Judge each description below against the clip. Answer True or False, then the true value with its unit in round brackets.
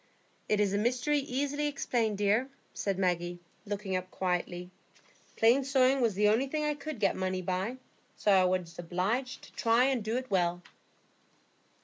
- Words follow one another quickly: False (165 wpm)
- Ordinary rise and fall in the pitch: False (5.7 semitones)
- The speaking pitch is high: True (210 Hz)